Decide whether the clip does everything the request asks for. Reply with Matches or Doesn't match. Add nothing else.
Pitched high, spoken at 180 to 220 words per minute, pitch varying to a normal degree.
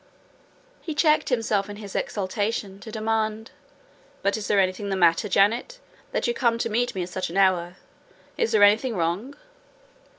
Doesn't match